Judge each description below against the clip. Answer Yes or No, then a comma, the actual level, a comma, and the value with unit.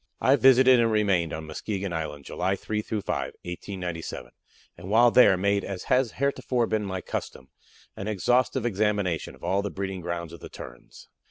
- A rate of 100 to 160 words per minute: No, average, 170 wpm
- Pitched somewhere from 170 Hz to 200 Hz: No, low, 100 Hz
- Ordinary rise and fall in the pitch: Yes, average, 4.4 semitones